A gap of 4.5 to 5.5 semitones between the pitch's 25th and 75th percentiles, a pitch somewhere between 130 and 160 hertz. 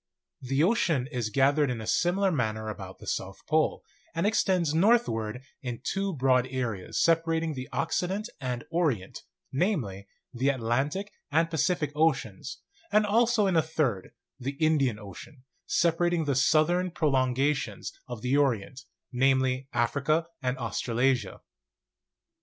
Yes: average, 4.9 semitones; medium, 140 Hz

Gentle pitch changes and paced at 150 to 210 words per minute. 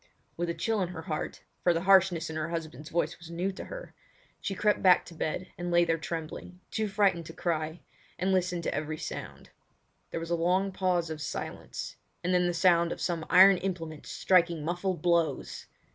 Yes: narrow, 2.1 semitones; average, 190 wpm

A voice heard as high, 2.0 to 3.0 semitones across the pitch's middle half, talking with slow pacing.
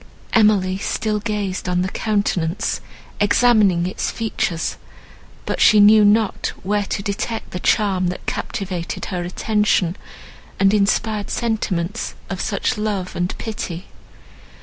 Yes: high, 200 Hz; average, 2.7 semitones; slow, 125 wpm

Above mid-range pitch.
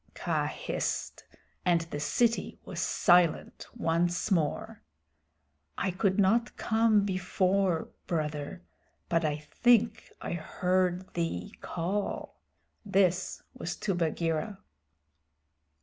No: medium, 180 Hz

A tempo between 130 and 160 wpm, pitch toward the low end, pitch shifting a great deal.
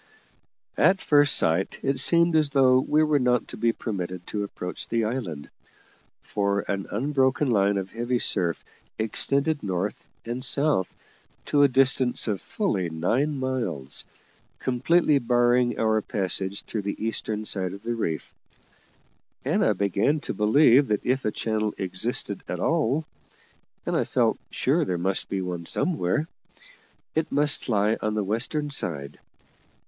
Yes: average, 150 wpm; low, 115 Hz; wide, 5.7 semitones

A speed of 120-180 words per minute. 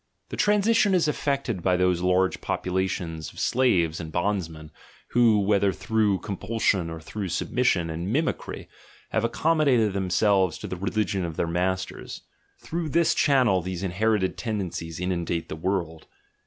Yes: average, 145 wpm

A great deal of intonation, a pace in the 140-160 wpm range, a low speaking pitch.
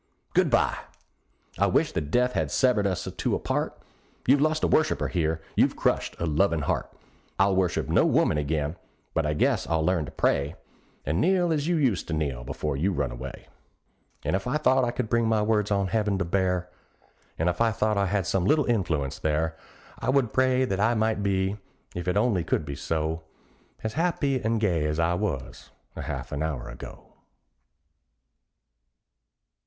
No: wide, 6.4 semitones; average, 185 wpm; very low, 95 Hz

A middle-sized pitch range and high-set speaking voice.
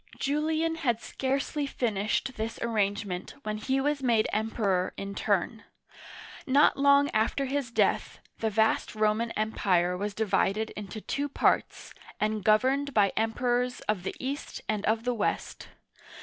Yes: average, 4.1 semitones; high, 225 Hz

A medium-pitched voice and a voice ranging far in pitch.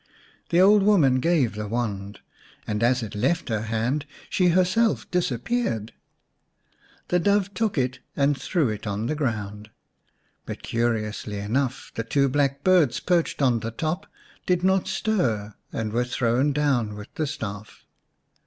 No: low, 130 Hz; wide, 7.7 semitones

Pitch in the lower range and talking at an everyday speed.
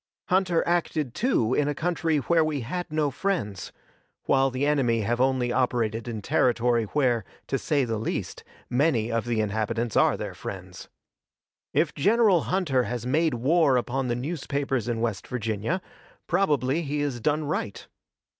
Yes: low, 130 Hz; average, 155 wpm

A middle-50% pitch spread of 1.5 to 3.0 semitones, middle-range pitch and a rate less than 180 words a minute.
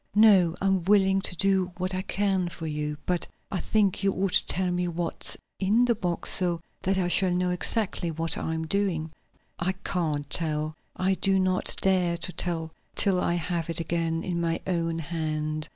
No: narrow, 2.5 semitones; medium, 180 Hz; average, 190 wpm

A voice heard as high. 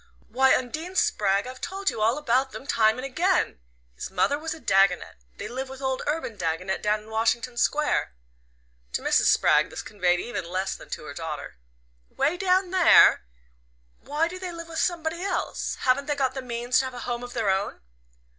Yes: very high, 255 Hz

